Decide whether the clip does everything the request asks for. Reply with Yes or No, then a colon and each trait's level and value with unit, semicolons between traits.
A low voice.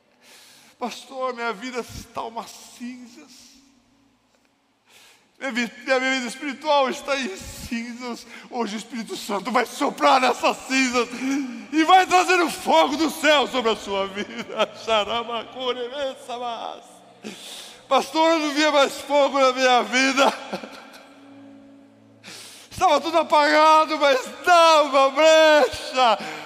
No: very high, 265 Hz